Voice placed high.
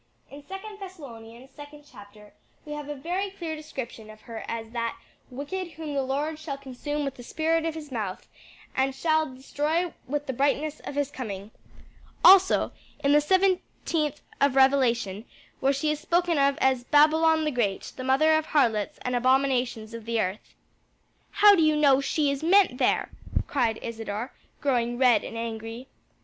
Yes: very high, 275 Hz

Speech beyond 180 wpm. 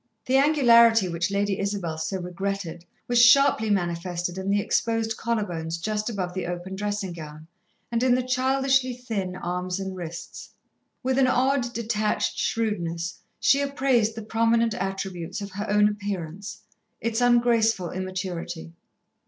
No: average, 145 wpm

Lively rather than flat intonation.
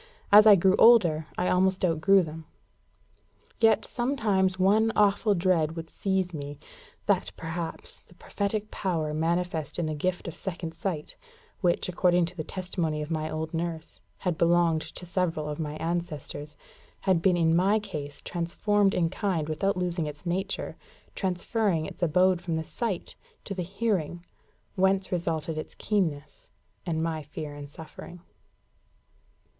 No: average, 3.1 semitones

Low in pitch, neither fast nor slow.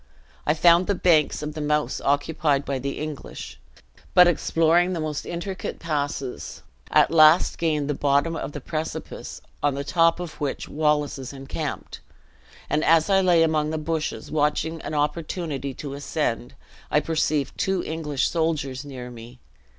No: medium, 150 Hz; average, 160 wpm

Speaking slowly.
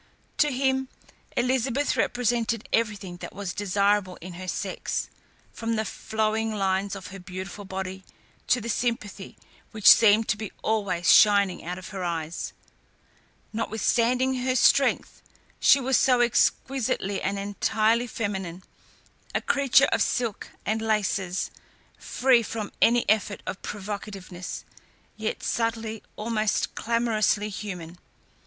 Yes: slow, 125 wpm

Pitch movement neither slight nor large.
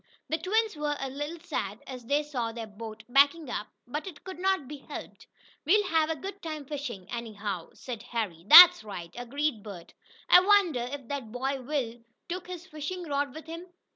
No: wide, 5.8 semitones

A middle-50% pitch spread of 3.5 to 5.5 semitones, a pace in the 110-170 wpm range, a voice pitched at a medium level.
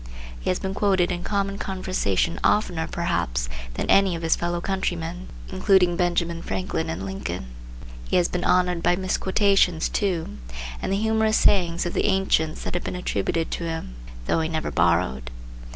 No: average, 2.9 semitones; average, 165 wpm; medium, 175 Hz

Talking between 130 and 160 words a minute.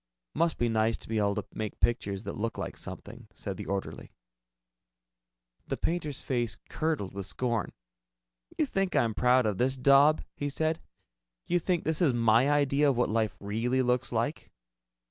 No: average, 170 wpm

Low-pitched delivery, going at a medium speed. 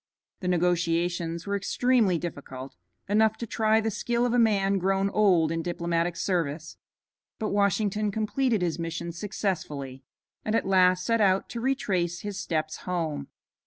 No: medium, 185 Hz; average, 150 wpm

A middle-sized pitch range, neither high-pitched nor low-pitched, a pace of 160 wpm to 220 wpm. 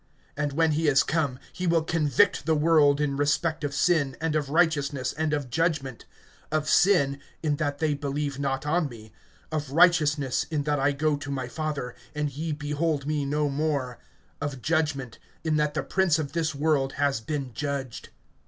No: narrow, 2.1 semitones; medium, 145 Hz; average, 180 wpm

